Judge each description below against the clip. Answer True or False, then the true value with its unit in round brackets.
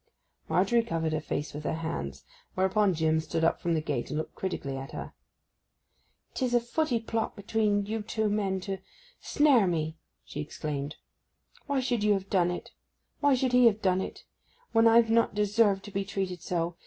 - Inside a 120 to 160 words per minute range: False (175 wpm)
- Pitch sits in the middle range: False (195 Hz)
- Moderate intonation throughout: False (5.7 semitones)